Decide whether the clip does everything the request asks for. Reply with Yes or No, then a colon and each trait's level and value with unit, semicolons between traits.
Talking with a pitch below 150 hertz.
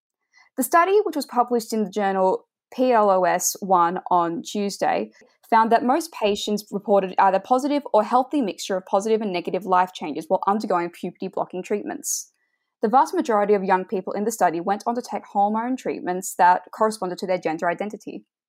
No: high, 205 Hz